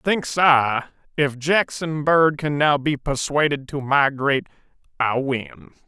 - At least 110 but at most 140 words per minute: Yes, slow, 135 wpm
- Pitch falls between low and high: Yes, medium, 145 Hz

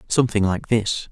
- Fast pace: No, average, 160 wpm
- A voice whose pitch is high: No, low, 110 Hz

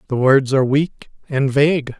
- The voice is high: No, medium, 140 Hz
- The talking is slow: No, average, 180 wpm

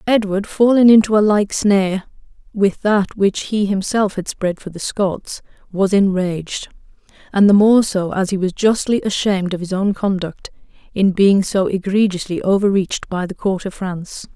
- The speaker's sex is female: Yes, female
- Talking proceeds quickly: No, average, 170 wpm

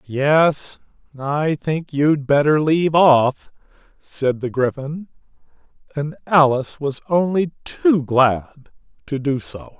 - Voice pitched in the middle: Yes, medium, 145 Hz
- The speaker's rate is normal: No, slow, 115 wpm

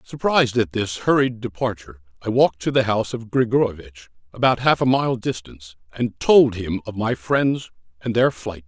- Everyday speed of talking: Yes, average, 180 wpm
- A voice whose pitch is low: Yes, low, 110 Hz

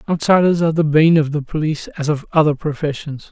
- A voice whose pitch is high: No, medium, 155 Hz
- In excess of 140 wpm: Yes, average, 200 wpm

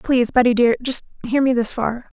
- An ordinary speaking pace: No, fast, 220 wpm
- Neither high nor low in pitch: No, high, 245 Hz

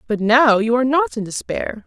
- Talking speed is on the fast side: Yes, fast, 225 wpm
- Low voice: No, high, 230 Hz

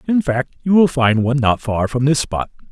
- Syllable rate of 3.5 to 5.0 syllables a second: Yes, 4.9 syllables/s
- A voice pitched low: Yes, low, 130 Hz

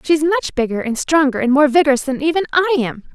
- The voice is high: Yes, very high, 290 Hz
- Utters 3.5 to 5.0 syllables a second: No, 6.5 syllables/s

